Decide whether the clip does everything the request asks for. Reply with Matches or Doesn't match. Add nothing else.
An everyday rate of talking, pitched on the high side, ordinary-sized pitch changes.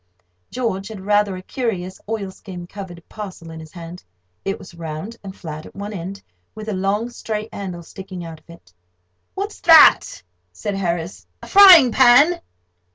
Matches